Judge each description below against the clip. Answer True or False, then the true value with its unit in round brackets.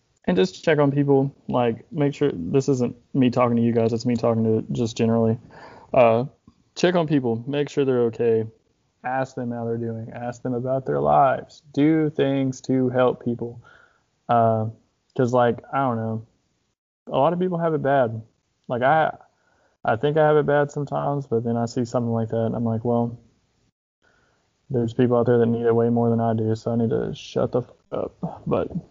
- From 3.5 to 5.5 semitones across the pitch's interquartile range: False (3.0 semitones)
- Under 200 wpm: False (205 wpm)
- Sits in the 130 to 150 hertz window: False (120 Hz)